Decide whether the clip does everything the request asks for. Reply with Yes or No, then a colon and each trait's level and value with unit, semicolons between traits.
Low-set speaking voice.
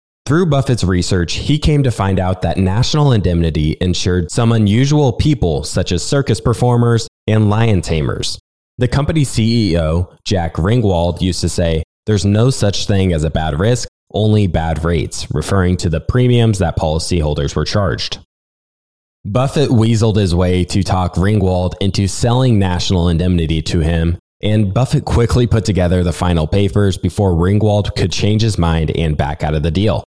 Yes: very low, 95 Hz